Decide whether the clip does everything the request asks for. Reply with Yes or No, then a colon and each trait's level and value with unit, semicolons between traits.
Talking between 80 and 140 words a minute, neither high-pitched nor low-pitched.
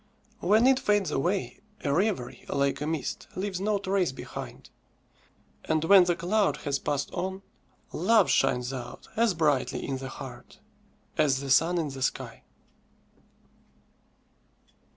Yes: slow, 135 wpm; medium, 165 Hz